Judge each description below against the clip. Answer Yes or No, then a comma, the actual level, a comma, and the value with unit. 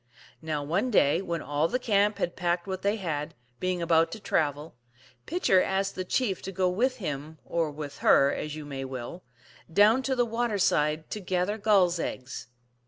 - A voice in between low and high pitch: Yes, medium, 180 Hz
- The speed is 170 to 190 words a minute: Yes, average, 185 wpm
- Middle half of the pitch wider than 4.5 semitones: Yes, average, 5.1 semitones